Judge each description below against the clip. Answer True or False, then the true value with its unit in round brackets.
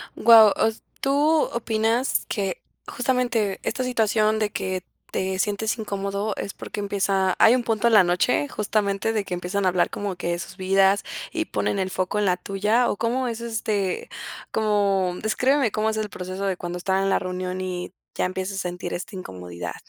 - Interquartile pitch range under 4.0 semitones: True (2.9 semitones)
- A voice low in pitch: False (200 Hz)